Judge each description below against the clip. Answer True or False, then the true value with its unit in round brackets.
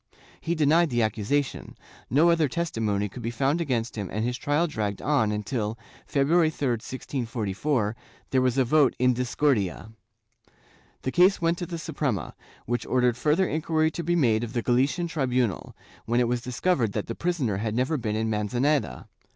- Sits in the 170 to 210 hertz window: False (125 Hz)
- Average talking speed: True (175 wpm)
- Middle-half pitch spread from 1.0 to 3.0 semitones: False (5.4 semitones)